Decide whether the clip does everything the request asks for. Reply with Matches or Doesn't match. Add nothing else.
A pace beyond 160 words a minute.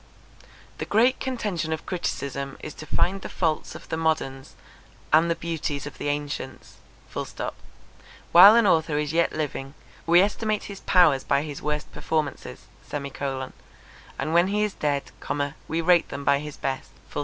Doesn't match